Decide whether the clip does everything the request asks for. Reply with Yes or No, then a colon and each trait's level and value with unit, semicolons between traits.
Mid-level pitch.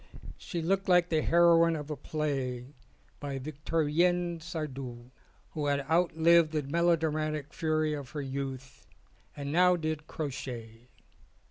Yes: medium, 155 Hz